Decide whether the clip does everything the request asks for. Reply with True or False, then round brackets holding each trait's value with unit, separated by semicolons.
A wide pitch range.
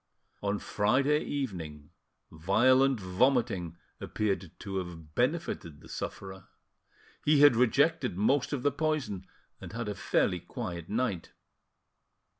True (6.8 semitones)